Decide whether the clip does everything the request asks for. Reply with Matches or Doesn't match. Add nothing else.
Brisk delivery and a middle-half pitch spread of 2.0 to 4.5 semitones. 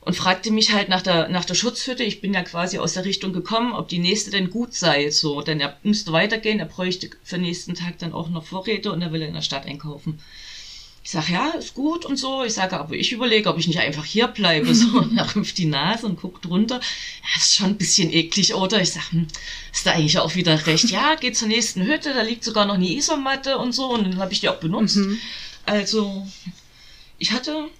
Doesn't match